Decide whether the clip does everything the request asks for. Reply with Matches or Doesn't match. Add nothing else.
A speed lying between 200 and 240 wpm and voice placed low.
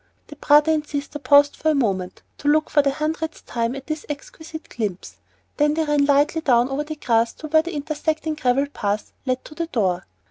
Doesn't match